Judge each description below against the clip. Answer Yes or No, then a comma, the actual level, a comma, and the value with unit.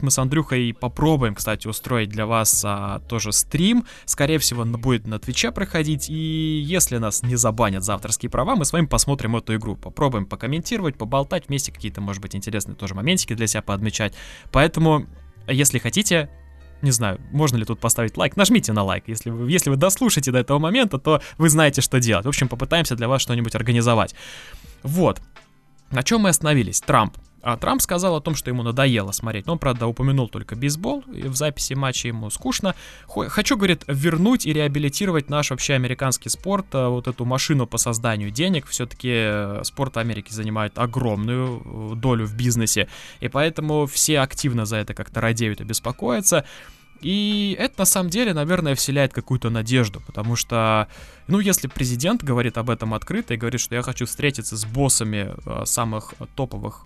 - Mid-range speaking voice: No, low, 125 Hz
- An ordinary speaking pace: No, fast, 175 wpm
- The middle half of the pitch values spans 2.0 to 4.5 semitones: No, average, 5.3 semitones